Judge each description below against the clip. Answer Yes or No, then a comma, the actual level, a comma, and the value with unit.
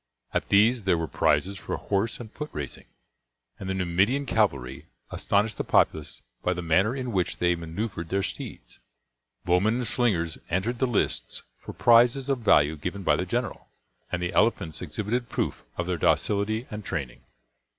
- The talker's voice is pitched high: No, low, 100 Hz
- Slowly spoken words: No, average, 170 wpm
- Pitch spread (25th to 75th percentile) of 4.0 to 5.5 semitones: Yes, average, 4.9 semitones